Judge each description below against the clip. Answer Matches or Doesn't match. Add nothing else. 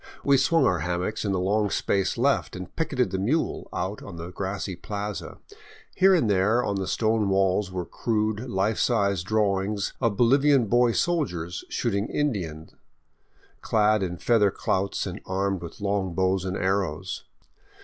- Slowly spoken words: Doesn't match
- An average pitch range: Matches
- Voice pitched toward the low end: Matches